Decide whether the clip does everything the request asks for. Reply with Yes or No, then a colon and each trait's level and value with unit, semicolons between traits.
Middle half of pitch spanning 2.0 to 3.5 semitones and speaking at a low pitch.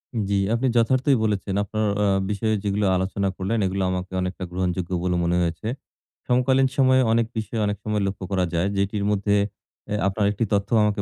Yes: average, 2.7 semitones; low, 100 Hz